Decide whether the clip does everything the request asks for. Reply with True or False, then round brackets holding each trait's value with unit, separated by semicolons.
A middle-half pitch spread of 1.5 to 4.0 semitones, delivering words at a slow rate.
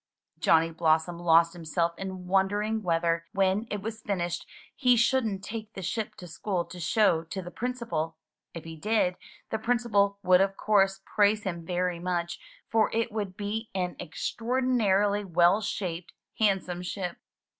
False (3.7 semitones; 155 wpm)